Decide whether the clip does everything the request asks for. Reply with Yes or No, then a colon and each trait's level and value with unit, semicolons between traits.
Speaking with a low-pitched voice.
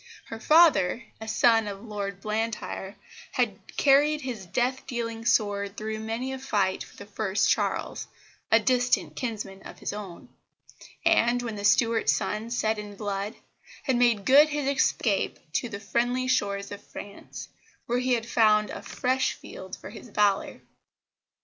No: high, 220 Hz